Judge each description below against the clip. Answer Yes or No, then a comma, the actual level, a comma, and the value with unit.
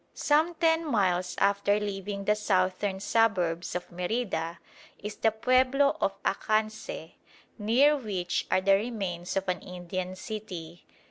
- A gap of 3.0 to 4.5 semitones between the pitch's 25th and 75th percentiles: Yes, average, 3.6 semitones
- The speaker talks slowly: Yes, slow, 130 wpm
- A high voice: Yes, high, 200 Hz